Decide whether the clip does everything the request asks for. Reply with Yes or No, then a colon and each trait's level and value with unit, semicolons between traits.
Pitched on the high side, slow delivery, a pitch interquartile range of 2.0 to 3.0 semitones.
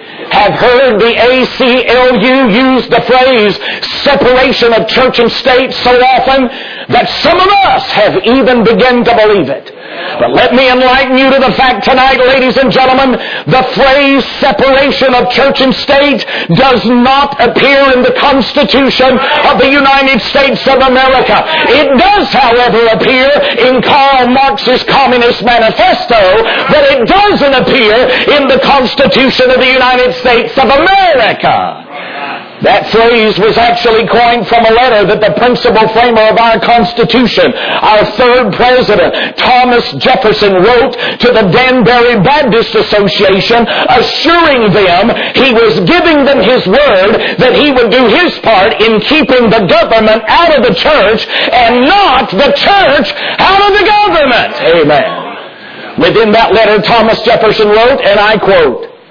No: very high, 250 Hz; average, 145 wpm; narrow, 2.6 semitones